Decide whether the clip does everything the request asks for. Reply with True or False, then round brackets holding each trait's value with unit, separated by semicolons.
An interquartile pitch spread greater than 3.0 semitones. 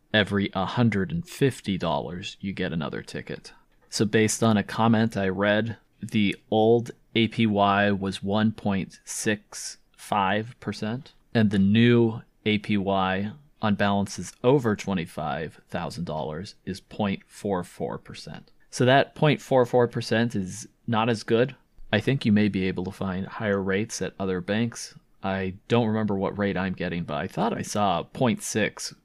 False (2.7 semitones)